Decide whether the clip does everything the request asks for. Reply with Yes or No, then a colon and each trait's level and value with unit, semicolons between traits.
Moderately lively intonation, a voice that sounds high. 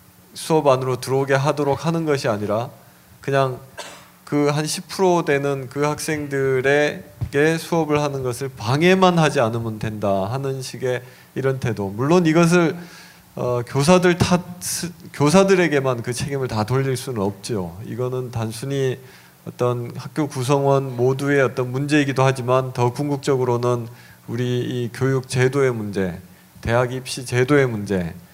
No: average, 3.1 semitones; low, 135 Hz